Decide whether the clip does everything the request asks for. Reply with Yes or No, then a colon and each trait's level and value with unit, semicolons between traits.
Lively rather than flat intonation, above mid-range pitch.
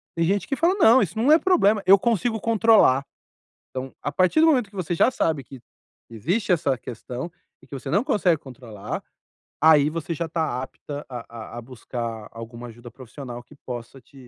No: wide, 8.7 semitones; medium, 150 Hz